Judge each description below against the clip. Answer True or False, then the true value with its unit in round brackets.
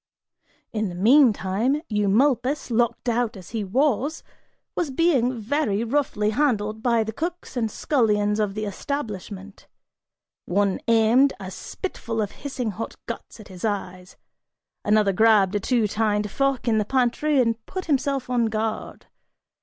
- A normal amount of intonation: True (4.1 semitones)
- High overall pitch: True (225 Hz)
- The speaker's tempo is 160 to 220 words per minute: False (145 wpm)